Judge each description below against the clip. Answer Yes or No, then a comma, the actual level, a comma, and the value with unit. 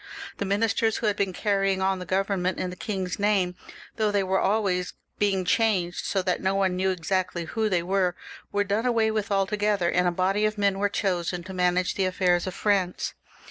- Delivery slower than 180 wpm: No, fast, 205 wpm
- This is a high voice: Yes, high, 195 Hz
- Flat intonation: Yes, narrow, 2.0 semitones